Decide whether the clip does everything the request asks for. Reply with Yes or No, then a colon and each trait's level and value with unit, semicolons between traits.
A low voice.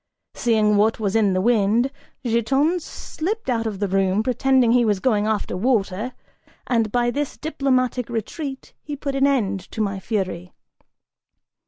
No: high, 230 Hz